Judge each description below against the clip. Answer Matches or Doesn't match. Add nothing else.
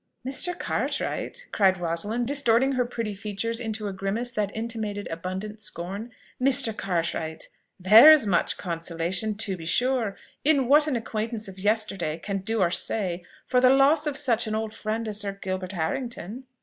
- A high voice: Matches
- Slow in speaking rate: Doesn't match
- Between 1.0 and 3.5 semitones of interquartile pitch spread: Doesn't match